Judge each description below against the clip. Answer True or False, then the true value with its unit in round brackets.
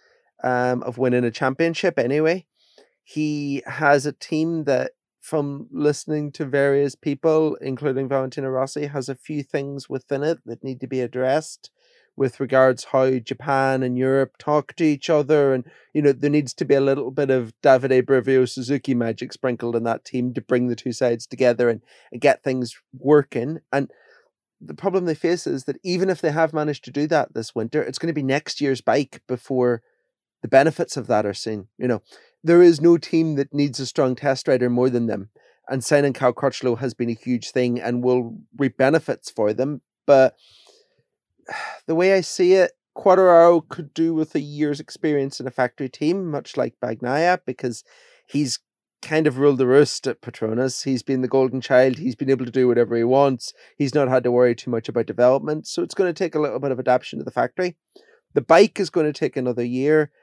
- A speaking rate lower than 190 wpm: False (200 wpm)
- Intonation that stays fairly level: False (3.4 semitones)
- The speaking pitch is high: False (135 Hz)